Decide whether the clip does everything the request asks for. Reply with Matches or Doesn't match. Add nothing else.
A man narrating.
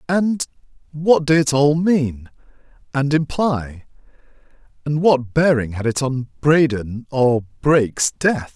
Matches